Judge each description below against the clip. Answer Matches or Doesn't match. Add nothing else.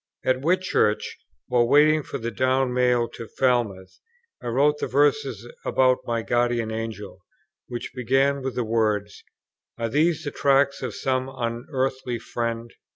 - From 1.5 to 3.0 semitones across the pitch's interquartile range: Matches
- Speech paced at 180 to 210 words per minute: Doesn't match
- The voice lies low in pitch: Matches